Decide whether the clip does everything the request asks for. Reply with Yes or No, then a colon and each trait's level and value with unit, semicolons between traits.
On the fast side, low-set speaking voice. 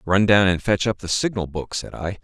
Yes: fast, 270 wpm; very low, 95 Hz